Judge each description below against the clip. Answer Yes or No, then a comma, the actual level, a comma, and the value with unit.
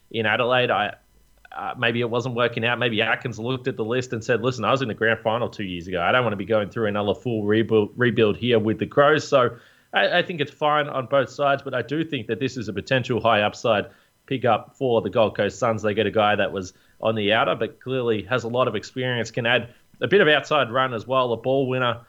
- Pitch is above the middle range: No, low, 120 Hz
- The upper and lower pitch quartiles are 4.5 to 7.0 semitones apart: No, average, 3.1 semitones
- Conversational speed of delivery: No, fast, 265 wpm